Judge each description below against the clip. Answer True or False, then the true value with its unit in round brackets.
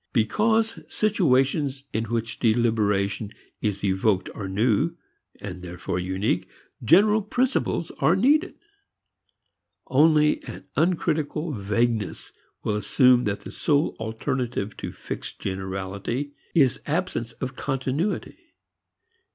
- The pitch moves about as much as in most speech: False (7.2 semitones)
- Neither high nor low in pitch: False (120 Hz)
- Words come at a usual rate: False (100 wpm)